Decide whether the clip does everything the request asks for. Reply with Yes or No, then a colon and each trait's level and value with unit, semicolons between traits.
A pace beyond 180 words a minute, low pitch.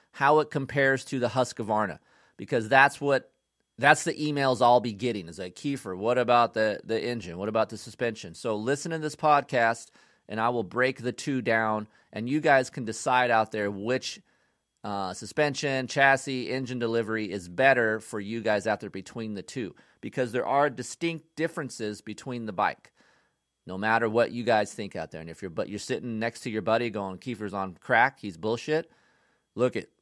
Yes: average, 190 wpm; low, 120 Hz